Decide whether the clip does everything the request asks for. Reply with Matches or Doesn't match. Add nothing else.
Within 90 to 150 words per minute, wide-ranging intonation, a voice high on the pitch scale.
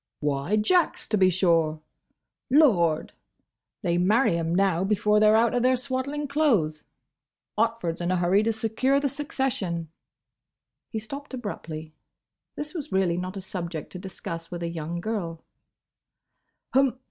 Matches